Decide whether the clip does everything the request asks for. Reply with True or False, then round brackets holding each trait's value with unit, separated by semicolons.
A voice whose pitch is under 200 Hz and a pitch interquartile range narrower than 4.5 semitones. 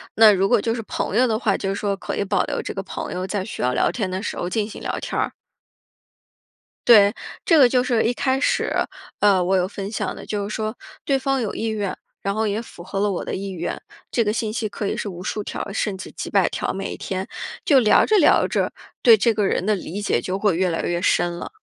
False (205 Hz; 2.8 semitones)